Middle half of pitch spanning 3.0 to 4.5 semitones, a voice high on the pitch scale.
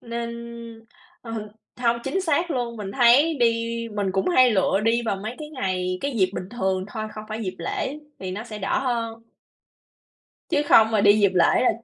Yes: average, 3.8 semitones; high, 225 Hz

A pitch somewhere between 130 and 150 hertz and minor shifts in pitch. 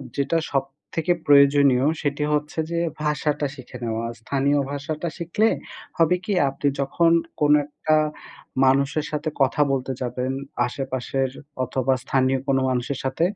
Yes: medium, 140 Hz; narrow, 2.2 semitones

